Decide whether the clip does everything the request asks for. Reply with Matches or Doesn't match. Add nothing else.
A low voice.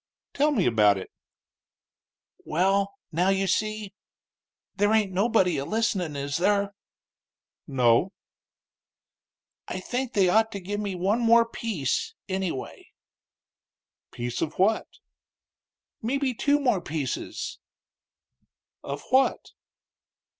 Doesn't match